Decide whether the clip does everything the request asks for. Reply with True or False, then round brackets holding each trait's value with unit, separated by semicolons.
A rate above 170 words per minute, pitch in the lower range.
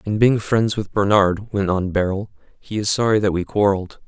True (205 wpm; 100 Hz)